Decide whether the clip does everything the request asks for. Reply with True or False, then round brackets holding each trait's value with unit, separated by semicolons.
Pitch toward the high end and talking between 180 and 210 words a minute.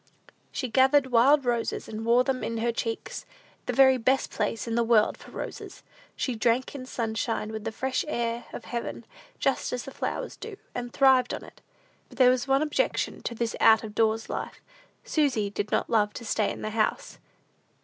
True (240 Hz; 195 wpm)